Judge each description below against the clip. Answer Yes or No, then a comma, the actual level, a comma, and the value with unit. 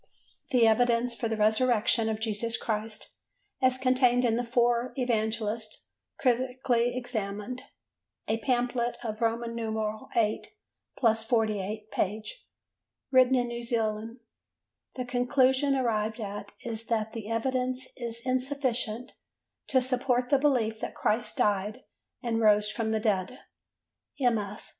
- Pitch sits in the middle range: No, high, 235 Hz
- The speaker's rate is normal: No, slow, 115 wpm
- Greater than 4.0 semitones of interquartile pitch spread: No, narrow, 2.4 semitones